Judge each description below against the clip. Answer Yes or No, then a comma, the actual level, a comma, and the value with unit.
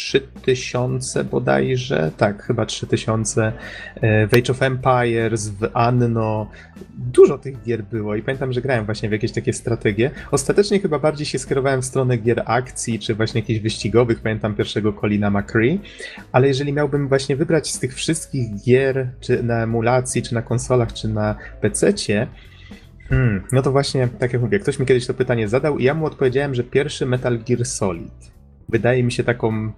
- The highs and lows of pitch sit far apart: No, average, 3.1 semitones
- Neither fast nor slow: No, fast, 170 wpm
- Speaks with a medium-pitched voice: No, low, 120 Hz